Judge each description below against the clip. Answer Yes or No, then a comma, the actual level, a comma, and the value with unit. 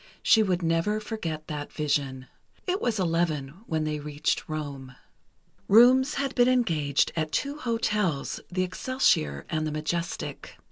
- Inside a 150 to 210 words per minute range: No, average, 140 wpm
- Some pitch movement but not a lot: No, wide, 6.7 semitones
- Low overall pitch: No, medium, 165 Hz